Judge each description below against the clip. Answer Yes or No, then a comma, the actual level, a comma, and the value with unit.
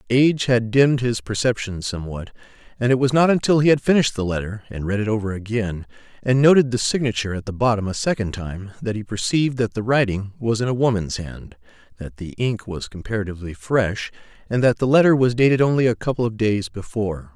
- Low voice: Yes, low, 115 Hz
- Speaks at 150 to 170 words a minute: No, fast, 205 wpm